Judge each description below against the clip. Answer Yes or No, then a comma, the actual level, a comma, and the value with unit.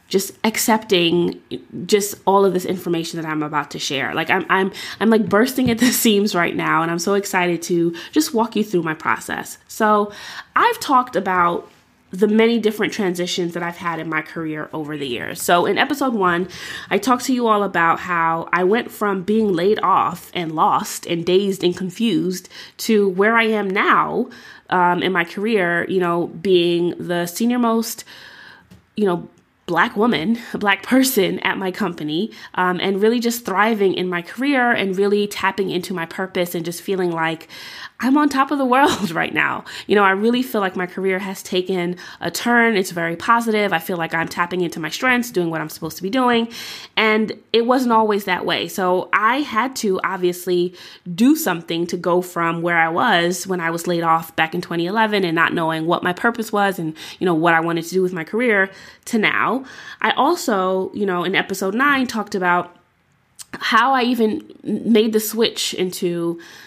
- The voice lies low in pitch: No, high, 190 Hz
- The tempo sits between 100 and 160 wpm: No, average, 195 wpm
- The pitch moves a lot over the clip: No, average, 4.0 semitones